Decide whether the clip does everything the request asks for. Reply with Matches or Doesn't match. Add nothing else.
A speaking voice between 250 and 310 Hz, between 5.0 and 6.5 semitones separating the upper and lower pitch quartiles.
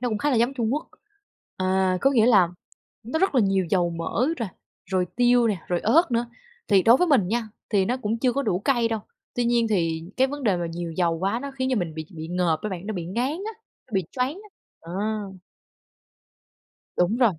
Doesn't match